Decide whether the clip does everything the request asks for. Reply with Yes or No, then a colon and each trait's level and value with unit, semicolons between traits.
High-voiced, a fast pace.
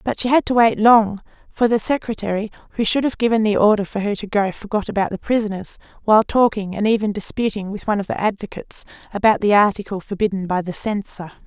Yes: high, 210 Hz; fast, 210 wpm